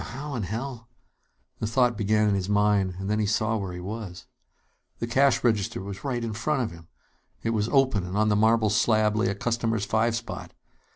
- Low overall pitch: Yes, low, 110 Hz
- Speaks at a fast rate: Yes, fast, 220 wpm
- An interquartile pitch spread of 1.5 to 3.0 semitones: Yes, narrow, 2.4 semitones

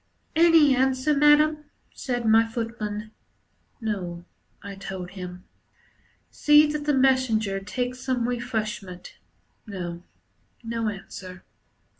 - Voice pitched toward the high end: Yes, high, 230 Hz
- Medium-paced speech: No, slow, 100 wpm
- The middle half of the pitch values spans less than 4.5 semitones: No, average, 5.1 semitones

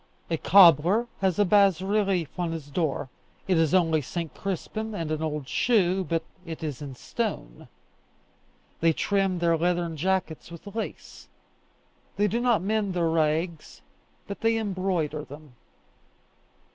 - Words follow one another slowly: No, average, 145 wpm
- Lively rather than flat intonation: No, average, 3.7 semitones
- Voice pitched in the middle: Yes, medium, 175 Hz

